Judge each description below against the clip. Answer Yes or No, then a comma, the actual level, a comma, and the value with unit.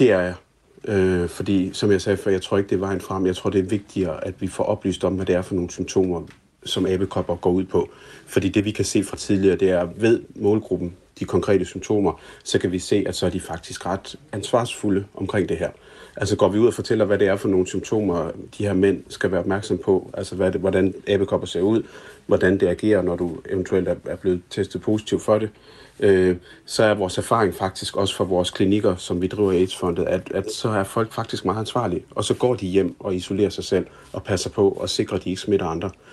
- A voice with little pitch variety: Yes, narrow, 2.1 semitones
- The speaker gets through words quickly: Yes, fast, 240 wpm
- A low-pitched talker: Yes, very low, 95 Hz